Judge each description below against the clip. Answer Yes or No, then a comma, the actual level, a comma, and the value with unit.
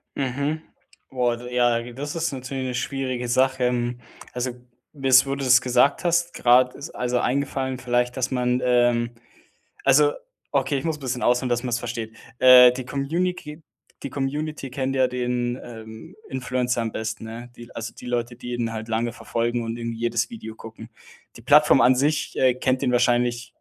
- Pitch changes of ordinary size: No, narrow, 1.9 semitones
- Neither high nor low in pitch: No, low, 125 Hz